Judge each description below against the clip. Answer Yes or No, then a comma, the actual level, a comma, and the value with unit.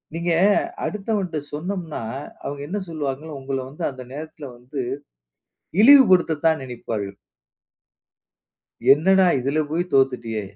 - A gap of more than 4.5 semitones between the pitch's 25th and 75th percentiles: Yes, average, 4.9 semitones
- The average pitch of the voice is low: No, medium, 150 Hz